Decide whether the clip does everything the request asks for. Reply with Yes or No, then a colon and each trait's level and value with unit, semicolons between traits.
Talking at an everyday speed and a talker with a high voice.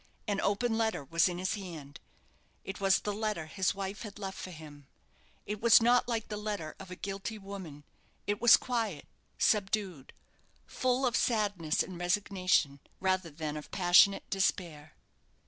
Yes: average, 160 wpm; high, 195 Hz